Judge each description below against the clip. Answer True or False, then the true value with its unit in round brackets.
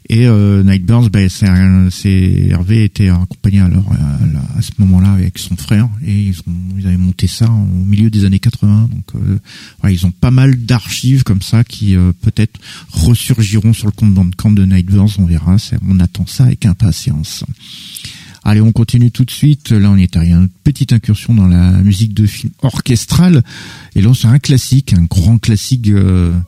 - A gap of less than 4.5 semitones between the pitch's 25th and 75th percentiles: True (3.7 semitones)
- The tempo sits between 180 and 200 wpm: False (210 wpm)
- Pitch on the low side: True (105 Hz)